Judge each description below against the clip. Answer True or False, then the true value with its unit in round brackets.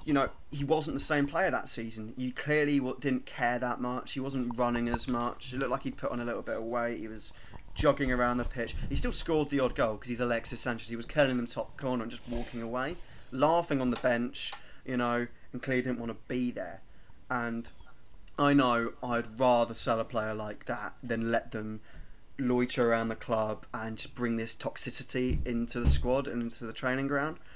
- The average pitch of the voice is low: True (120 Hz)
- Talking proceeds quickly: True (220 wpm)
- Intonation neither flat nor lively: False (2.0 semitones)